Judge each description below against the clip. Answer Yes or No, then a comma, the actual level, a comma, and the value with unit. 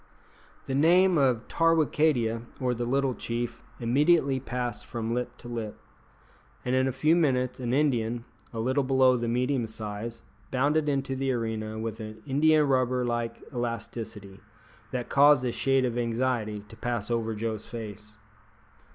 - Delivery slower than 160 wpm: Yes, average, 150 wpm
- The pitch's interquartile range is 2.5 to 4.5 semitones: Yes, average, 2.8 semitones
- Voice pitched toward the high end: No, low, 120 Hz